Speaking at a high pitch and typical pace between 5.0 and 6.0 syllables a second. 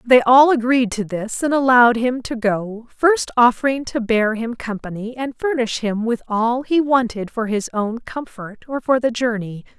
No: high, 240 Hz; 4.5 syllables/s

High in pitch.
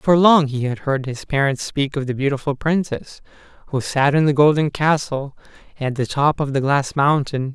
No: medium, 140 Hz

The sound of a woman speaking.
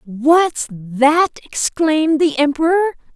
Yes: female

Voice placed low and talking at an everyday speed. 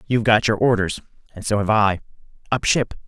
Yes: low, 110 Hz; average, 195 wpm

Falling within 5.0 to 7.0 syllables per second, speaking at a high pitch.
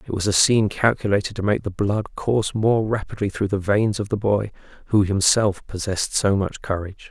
No: 5.5 syllables/s; low, 100 Hz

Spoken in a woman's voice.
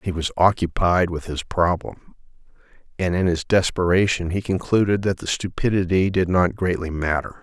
No: male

